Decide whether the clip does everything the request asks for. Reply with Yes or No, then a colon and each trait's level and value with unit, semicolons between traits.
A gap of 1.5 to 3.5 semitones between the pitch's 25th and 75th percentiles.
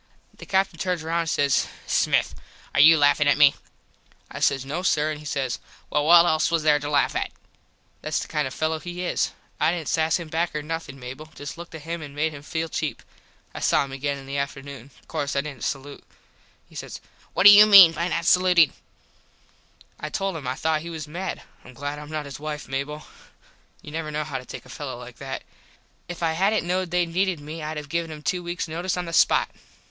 Yes: average, 2.8 semitones